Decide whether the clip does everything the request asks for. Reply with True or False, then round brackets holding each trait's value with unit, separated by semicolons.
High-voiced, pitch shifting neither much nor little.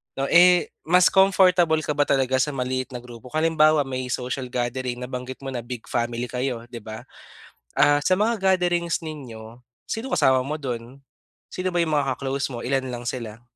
False (135 Hz; 4.3 semitones)